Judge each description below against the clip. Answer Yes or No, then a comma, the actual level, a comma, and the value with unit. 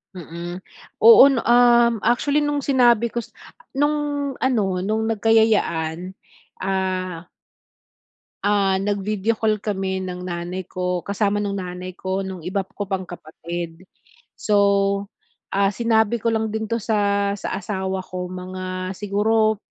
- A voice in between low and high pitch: No, high, 200 Hz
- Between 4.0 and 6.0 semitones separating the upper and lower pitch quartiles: No, average, 3.4 semitones